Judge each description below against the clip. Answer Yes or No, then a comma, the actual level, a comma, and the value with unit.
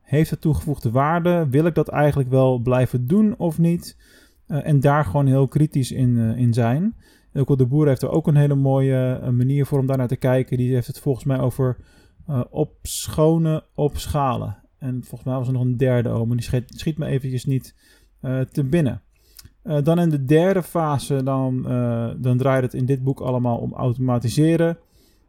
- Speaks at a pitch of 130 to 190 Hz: Yes, low, 135 Hz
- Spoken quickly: Yes, fast, 205 wpm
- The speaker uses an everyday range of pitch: Yes, average, 3.1 semitones